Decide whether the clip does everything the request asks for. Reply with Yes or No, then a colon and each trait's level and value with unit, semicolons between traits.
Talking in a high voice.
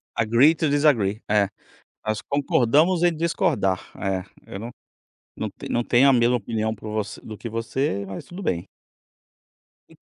No: low, 115 Hz